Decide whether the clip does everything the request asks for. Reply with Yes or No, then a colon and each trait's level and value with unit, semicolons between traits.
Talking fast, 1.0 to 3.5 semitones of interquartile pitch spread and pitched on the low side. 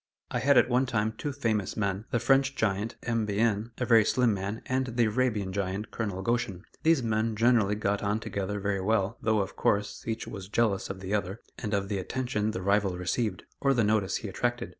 Yes: fast, 210 wpm; average, 3.0 semitones; low, 105 Hz